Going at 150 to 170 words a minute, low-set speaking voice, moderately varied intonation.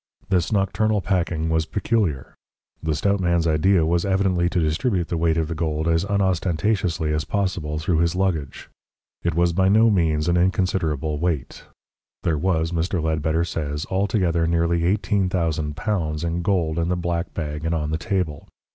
Yes: average, 165 wpm; very low, 85 Hz; average, 3.0 semitones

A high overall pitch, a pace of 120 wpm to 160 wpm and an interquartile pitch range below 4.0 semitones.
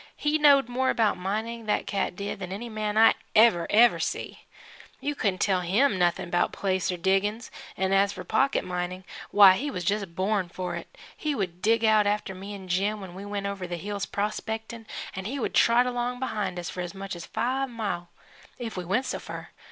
No: high, 200 Hz; fast, 205 wpm; average, 3.6 semitones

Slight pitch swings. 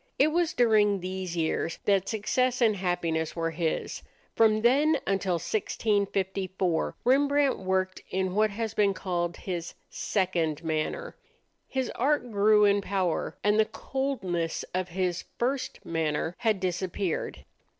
No: average, 4.0 semitones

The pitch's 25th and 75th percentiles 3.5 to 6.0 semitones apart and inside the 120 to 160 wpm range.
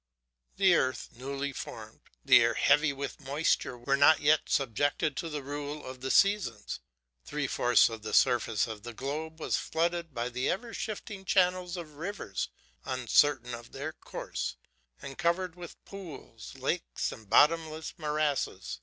Yes: average, 4.5 semitones; average, 155 wpm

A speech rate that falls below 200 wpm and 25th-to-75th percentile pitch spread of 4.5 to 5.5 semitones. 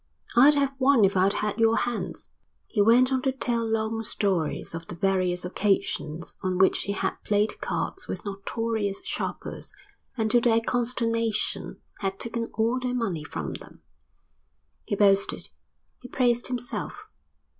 No: average, 150 wpm; average, 3.7 semitones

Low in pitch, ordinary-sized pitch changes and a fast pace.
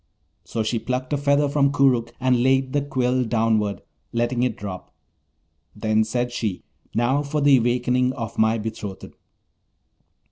No: low, 125 Hz; average, 3.0 semitones; average, 145 wpm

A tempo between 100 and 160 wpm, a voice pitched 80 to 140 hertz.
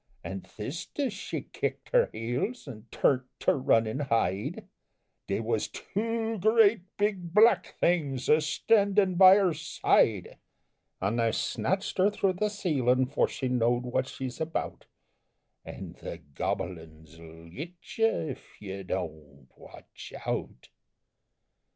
Yes: average, 140 wpm; low, 135 Hz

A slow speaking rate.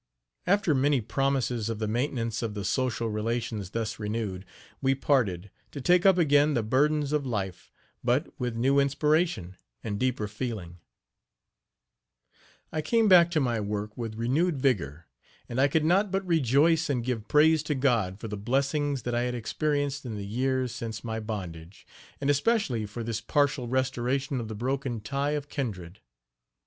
No: average, 165 wpm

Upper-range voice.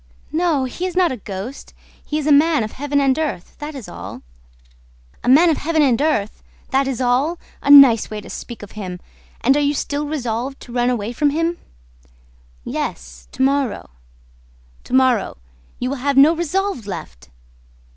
Yes: very high, 270 Hz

